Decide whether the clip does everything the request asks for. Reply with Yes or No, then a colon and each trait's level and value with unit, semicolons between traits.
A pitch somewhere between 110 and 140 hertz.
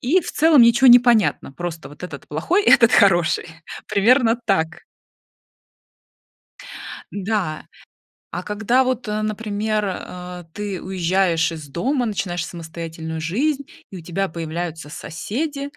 No: high, 195 Hz